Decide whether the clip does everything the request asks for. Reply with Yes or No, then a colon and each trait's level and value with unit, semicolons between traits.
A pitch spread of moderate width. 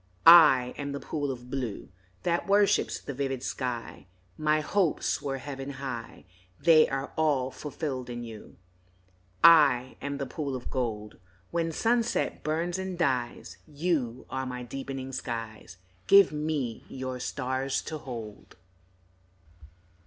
Yes: average, 3.6 semitones